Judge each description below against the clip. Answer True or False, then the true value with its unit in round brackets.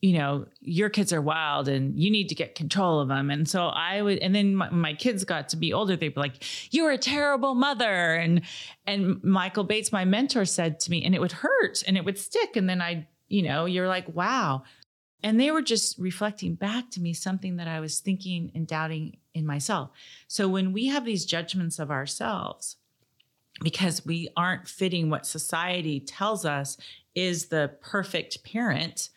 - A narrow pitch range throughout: False (4.0 semitones)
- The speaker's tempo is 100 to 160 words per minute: False (195 wpm)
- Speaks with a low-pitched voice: False (175 Hz)